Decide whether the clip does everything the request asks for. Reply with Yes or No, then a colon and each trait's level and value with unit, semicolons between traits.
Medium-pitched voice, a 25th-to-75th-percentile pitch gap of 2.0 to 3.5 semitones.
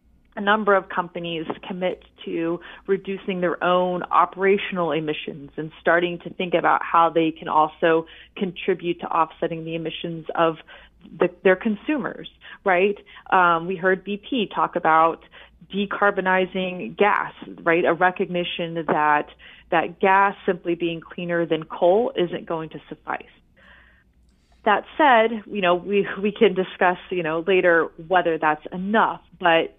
Yes: medium, 175 Hz; average, 2.8 semitones